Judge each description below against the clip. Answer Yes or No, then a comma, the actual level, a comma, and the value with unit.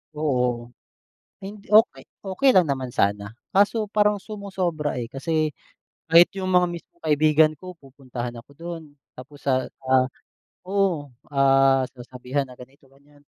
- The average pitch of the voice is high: No, medium, 145 Hz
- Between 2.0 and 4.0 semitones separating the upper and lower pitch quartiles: No, wide, 5.4 semitones